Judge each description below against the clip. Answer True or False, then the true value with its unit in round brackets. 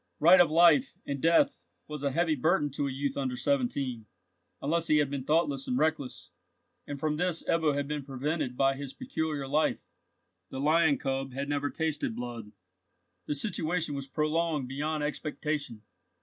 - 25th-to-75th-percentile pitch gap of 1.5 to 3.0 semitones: True (2.7 semitones)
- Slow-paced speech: False (165 wpm)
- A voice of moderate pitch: True (145 Hz)